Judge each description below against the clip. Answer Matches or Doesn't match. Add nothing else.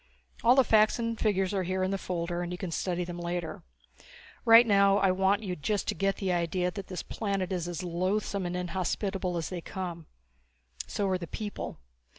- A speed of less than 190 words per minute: Doesn't match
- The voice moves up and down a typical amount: Doesn't match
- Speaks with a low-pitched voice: Doesn't match